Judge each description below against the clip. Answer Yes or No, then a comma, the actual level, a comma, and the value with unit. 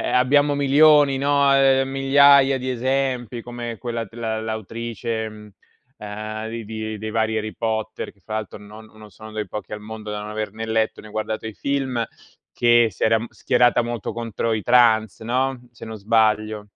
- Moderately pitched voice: No, low, 115 Hz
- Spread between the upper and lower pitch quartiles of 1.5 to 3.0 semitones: Yes, narrow, 2.6 semitones